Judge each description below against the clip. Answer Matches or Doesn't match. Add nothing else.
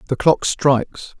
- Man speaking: Matches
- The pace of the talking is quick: Doesn't match